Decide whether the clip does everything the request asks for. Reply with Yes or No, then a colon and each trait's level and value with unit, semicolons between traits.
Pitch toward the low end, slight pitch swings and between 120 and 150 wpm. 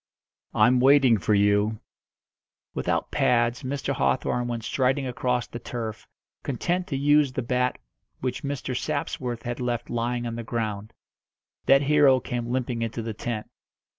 Yes: low, 125 Hz; narrow, 2.3 semitones; average, 145 wpm